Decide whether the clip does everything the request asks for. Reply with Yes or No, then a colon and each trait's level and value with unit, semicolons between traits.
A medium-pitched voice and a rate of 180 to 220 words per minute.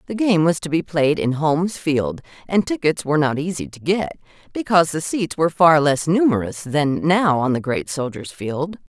Yes: medium, 155 Hz; average, 200 wpm